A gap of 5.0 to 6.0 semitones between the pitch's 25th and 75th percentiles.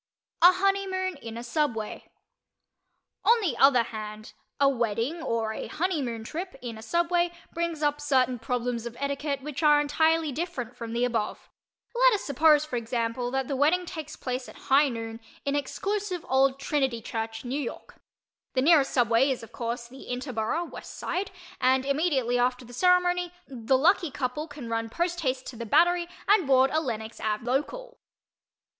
Yes: wide, 5.5 semitones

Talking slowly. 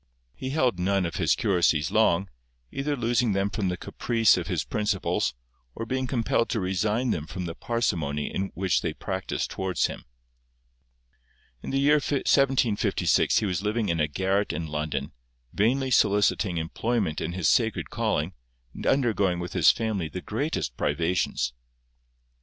No: average, 155 wpm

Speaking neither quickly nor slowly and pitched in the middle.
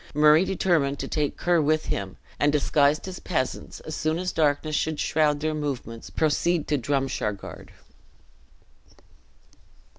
No: slow, 130 wpm; medium, 150 Hz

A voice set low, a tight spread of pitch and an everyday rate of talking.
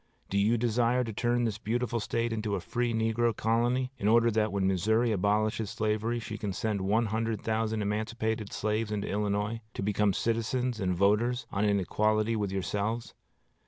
Yes: low, 110 Hz; narrow, 2.0 semitones; average, 175 wpm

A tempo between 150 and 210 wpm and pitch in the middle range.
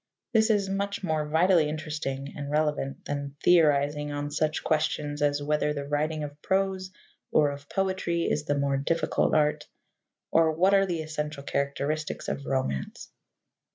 Yes: average, 155 wpm; medium, 150 Hz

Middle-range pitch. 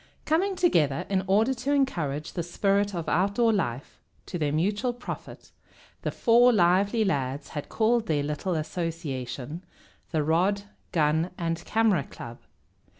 Yes: medium, 180 Hz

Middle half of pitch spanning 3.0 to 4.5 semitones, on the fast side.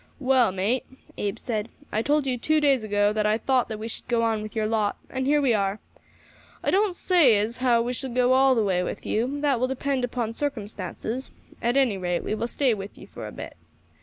Yes: average, 3.7 semitones; fast, 230 wpm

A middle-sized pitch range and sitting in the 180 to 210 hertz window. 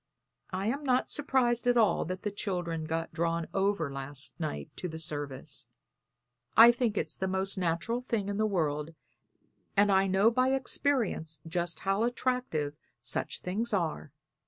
No: wide, 6.0 semitones; high, 190 Hz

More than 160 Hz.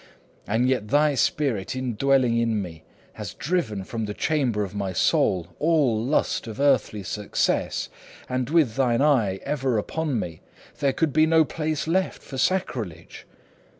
No: low, 130 Hz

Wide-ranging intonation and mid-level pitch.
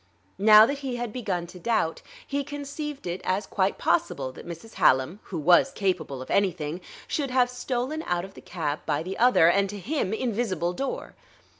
No: wide, 6.5 semitones; high, 200 Hz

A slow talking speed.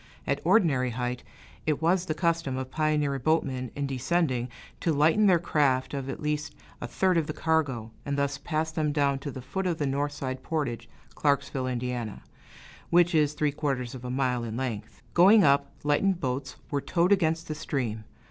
No: average, 185 wpm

